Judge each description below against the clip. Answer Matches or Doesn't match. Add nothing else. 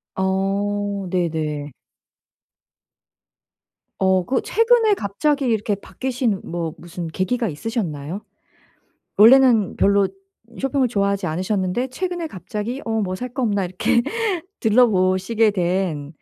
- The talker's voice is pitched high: Matches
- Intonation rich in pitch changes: Doesn't match